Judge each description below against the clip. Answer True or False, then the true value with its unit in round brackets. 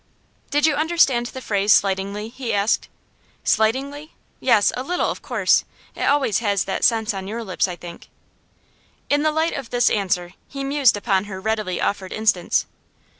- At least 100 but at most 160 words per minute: False (170 wpm)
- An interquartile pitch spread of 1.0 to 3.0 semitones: False (5.5 semitones)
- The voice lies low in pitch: False (220 Hz)